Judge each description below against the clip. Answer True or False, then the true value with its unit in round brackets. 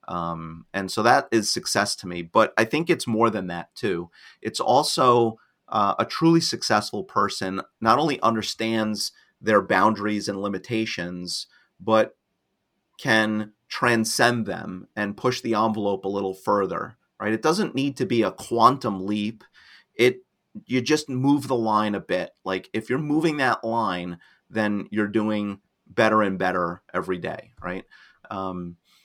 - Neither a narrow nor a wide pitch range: True (3.9 semitones)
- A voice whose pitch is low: True (110 Hz)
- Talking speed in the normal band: True (155 wpm)